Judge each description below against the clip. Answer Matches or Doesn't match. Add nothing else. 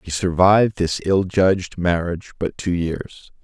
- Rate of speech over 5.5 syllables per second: Doesn't match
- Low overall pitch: Matches